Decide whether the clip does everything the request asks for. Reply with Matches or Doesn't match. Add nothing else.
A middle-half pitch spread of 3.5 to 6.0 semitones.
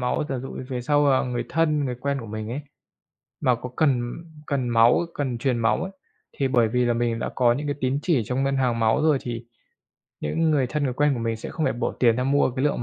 Doesn't match